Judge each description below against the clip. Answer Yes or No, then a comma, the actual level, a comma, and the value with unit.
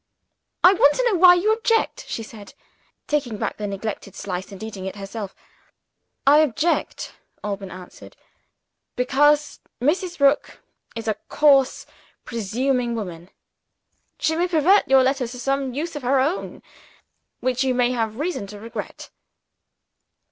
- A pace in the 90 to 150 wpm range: Yes, average, 140 wpm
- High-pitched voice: Yes, very high, 255 Hz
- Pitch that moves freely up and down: Yes, wide, 5.7 semitones